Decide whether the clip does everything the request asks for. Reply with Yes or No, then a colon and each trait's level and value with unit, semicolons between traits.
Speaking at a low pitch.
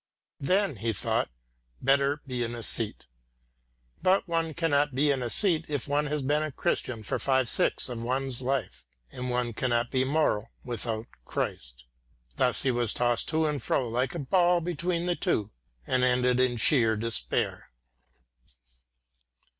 Yes: low, 130 Hz